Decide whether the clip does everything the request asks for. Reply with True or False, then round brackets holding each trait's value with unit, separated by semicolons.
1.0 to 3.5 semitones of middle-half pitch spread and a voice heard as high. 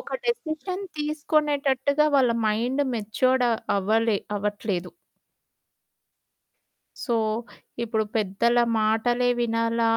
False (4.5 semitones; 235 Hz)